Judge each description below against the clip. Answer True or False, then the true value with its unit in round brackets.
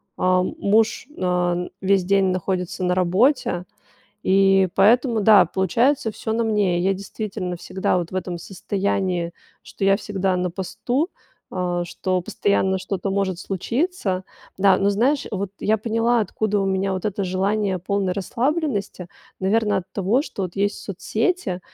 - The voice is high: True (195 Hz)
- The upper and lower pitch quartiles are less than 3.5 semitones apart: True (2.7 semitones)